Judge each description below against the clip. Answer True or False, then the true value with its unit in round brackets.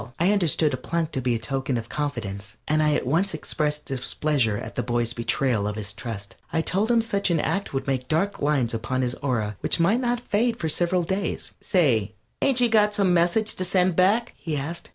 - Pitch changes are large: True (7.6 semitones)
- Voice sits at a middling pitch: True (150 Hz)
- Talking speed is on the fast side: True (215 wpm)